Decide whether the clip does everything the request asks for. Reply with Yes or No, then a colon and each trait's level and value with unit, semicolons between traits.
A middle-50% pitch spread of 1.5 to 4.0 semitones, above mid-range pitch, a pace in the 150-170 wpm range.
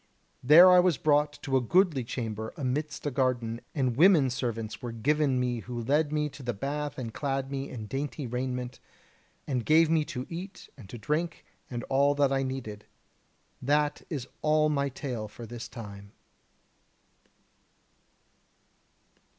No: average, 3.7 semitones; low, 135 Hz; average, 155 wpm